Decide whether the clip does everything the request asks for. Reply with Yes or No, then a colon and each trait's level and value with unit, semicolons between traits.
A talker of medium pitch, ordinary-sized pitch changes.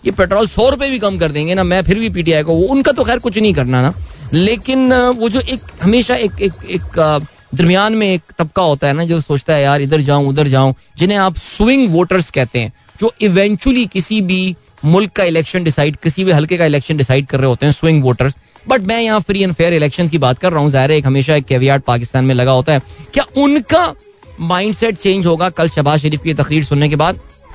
No: medium, 170 Hz; wide, 6.2 semitones